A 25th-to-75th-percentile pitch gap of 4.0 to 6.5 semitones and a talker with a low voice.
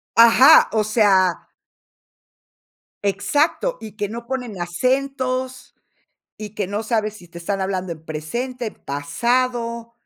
No: average, 4.9 semitones; high, 220 Hz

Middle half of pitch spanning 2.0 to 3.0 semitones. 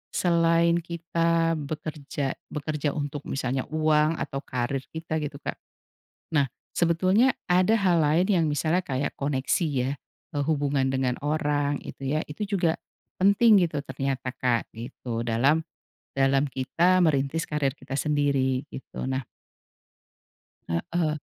No: average, 3.5 semitones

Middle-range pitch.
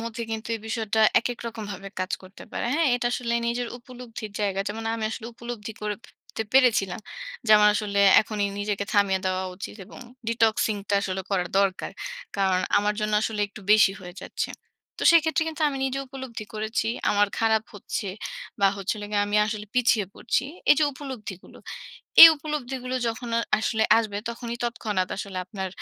No: high, 220 Hz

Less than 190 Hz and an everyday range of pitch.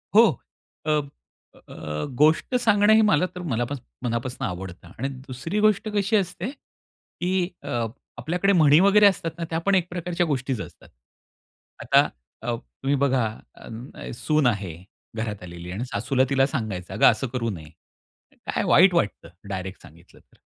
No: medium, 140 Hz; wide, 7.8 semitones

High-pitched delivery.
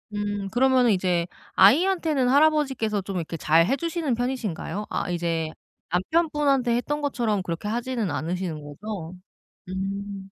Yes: high, 210 Hz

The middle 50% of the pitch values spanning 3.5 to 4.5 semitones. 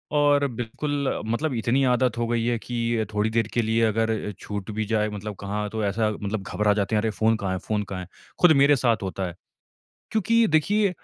No: average, 3.1 semitones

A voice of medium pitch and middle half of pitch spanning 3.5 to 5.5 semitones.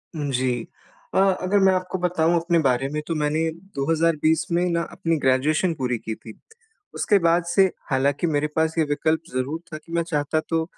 No: medium, 160 Hz; average, 3.0 semitones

